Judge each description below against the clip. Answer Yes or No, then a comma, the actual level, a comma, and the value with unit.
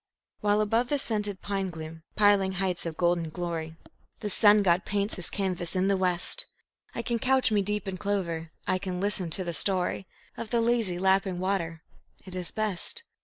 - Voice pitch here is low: No, high, 190 Hz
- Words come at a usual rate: Yes, average, 185 wpm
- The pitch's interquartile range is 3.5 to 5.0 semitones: No, average, 2.8 semitones